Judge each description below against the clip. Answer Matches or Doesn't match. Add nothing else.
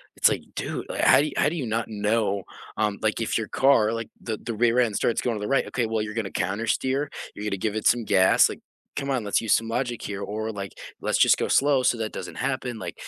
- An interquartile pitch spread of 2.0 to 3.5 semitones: Matches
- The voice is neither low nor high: Doesn't match